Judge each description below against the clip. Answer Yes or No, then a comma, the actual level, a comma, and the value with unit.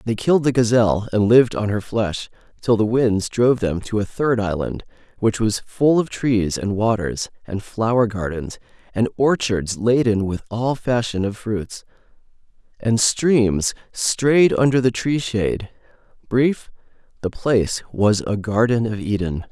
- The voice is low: Yes, low, 110 Hz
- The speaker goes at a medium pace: Yes, average, 155 wpm